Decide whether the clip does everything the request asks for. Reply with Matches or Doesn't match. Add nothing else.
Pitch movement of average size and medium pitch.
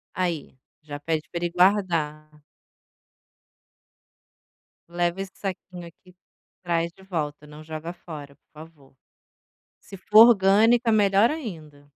Matches